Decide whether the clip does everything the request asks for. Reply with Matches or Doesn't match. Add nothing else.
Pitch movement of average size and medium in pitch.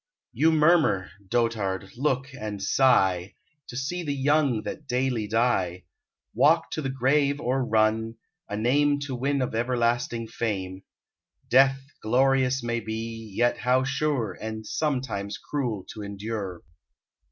Doesn't match